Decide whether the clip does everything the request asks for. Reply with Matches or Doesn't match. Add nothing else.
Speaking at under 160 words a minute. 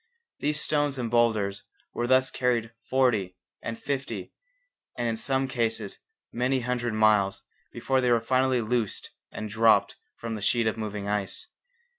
Matches